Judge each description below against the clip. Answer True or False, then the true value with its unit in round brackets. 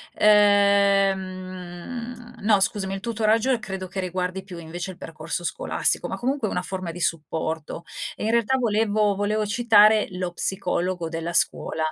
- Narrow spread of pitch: False (3.2 semitones)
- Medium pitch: False (195 Hz)